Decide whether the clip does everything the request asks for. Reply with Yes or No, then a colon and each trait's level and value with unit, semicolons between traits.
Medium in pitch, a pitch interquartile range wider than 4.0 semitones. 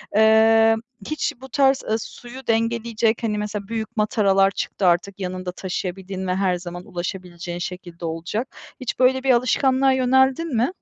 No: high, 220 Hz; average, 5.0 semitones